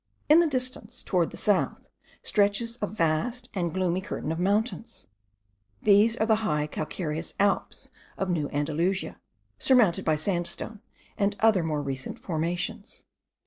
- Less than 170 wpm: Yes, average, 140 wpm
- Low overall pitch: No, high, 195 Hz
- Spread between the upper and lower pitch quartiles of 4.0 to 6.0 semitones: Yes, average, 5.1 semitones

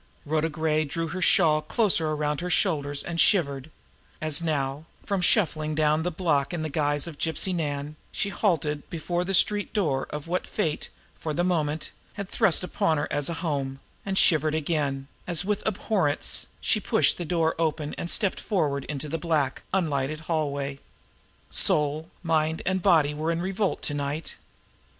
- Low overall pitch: No, medium, 155 Hz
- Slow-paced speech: No, average, 170 wpm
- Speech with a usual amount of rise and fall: Yes, average, 3.0 semitones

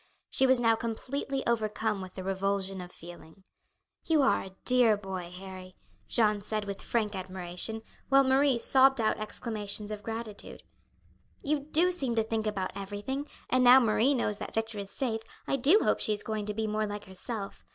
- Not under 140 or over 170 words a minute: No, average, 185 wpm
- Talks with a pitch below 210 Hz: No, high, 215 Hz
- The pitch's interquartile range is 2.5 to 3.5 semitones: No, average, 4.0 semitones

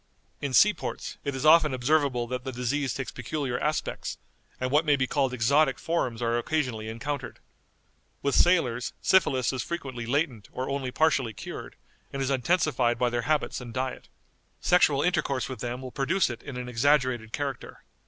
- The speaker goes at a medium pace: Yes, average, 175 wpm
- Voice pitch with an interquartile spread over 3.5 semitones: No, average, 3.1 semitones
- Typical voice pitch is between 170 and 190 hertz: No, low, 130 Hz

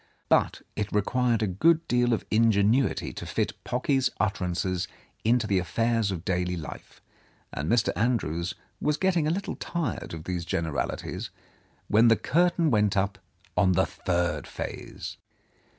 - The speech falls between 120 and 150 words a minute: Yes, average, 145 wpm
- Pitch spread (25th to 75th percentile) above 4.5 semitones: Yes, average, 5.3 semitones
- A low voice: Yes, low, 110 Hz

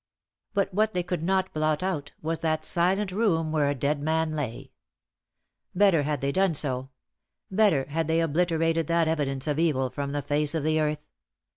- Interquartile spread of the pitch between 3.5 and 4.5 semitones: No, average, 3.1 semitones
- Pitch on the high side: No, medium, 160 Hz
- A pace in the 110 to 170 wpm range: No, average, 180 wpm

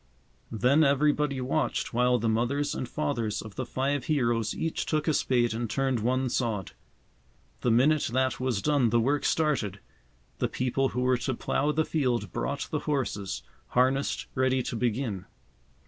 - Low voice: Yes, low, 130 Hz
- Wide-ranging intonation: No, average, 3.2 semitones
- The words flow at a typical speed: Yes, average, 165 wpm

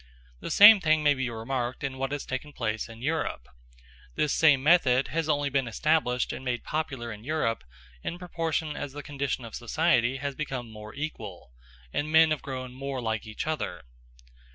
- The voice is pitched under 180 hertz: Yes, low, 135 Hz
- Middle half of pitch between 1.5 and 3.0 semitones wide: No, average, 4.2 semitones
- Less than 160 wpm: No, average, 180 wpm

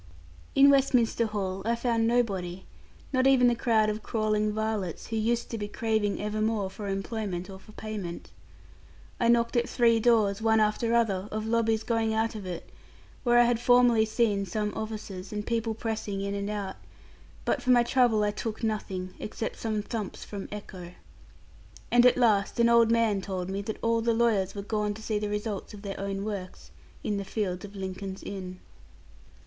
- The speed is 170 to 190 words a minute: Yes, average, 185 wpm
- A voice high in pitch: Yes, high, 215 Hz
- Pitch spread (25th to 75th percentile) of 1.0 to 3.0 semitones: Yes, narrow, 2.5 semitones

